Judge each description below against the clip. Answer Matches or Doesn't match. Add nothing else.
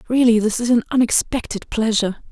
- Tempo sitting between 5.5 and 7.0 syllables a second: Matches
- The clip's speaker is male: Doesn't match